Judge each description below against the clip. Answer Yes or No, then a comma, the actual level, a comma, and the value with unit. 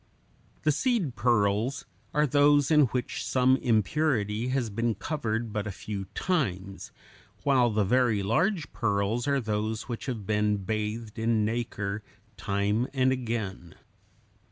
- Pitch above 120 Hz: No, low, 115 Hz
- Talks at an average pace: No, slow, 130 wpm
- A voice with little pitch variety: No, average, 3.9 semitones